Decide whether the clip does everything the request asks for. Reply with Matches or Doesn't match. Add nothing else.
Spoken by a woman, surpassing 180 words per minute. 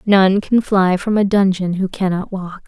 Matches